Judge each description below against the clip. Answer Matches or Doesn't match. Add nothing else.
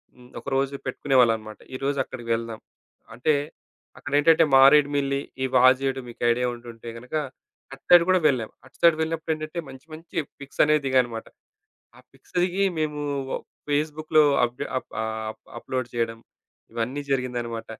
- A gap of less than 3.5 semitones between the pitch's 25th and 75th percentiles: Doesn't match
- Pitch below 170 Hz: Matches